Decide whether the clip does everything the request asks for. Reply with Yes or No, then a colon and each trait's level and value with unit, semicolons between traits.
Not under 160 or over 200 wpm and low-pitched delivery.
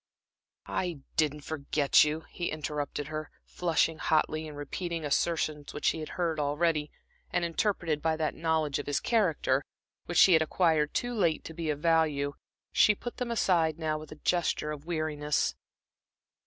No: average, 165 wpm; medium, 155 Hz